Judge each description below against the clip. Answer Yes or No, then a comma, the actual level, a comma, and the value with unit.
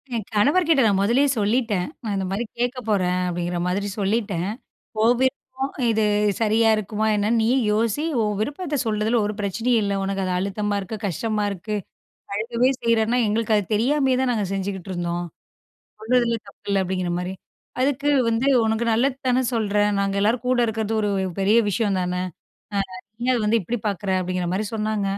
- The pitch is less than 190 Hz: No, high, 215 Hz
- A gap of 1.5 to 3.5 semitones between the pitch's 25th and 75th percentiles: Yes, average, 3.2 semitones